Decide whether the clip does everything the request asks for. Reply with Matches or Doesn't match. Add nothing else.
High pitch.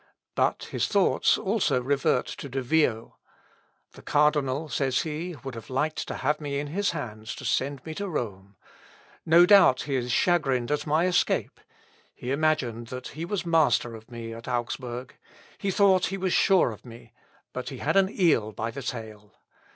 Doesn't match